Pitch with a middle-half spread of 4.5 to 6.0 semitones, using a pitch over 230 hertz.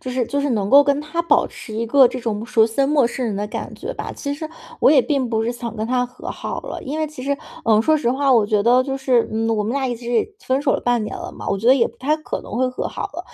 No: average, 3.6 semitones; very high, 250 Hz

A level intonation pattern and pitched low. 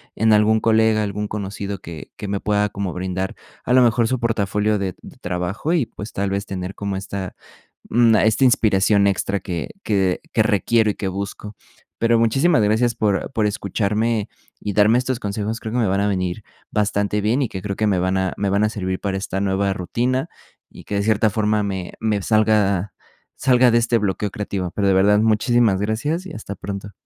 Yes: narrow, 2.2 semitones; low, 105 Hz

